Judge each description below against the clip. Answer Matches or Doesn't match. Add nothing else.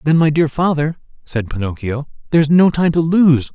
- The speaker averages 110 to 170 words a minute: Doesn't match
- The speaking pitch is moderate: Matches